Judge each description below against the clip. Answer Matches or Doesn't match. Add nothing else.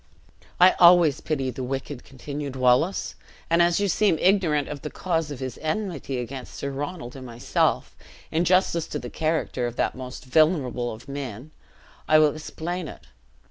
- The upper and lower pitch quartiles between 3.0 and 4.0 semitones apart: Doesn't match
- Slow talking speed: Doesn't match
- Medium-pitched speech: Matches